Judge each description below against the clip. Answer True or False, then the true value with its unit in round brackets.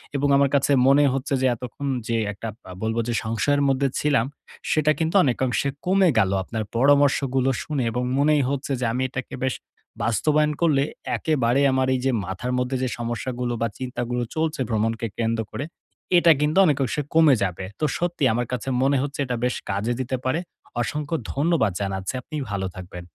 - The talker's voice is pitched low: True (130 Hz)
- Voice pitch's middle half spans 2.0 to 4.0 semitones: True (3.7 semitones)